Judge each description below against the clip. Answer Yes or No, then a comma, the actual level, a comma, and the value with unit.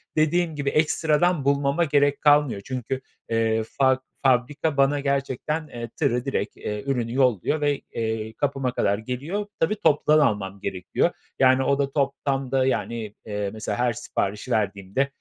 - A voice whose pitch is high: No, low, 135 Hz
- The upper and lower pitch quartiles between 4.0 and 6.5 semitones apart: Yes, average, 4.3 semitones